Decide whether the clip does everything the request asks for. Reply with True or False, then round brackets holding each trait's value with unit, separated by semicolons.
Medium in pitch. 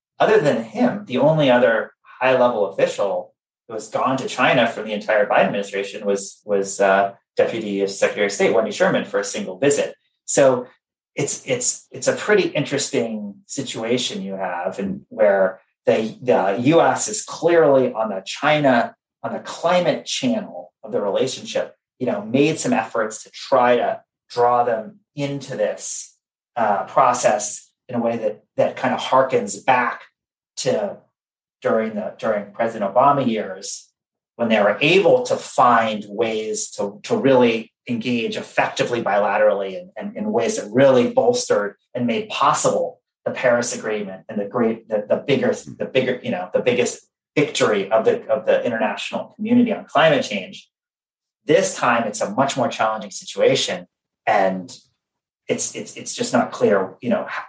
True (165 Hz)